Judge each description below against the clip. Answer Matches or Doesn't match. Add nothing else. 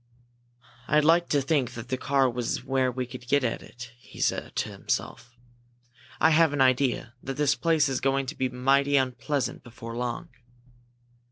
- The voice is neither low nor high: Doesn't match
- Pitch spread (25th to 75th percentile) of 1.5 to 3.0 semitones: Matches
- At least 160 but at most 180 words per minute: Matches